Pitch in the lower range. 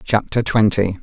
Yes: low, 105 Hz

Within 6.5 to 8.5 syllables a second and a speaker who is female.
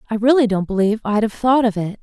Yes: 6.8 syllables/s; female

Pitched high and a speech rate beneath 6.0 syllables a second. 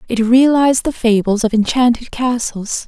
Yes: high, 240 Hz; 4.8 syllables/s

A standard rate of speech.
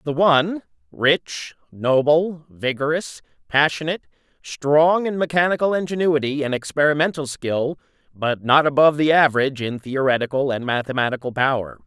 No: slow, 115 wpm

